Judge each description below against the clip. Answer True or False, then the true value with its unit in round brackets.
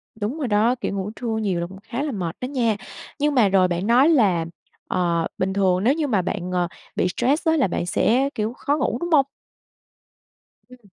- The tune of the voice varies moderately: False (6.1 semitones)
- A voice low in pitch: False (220 Hz)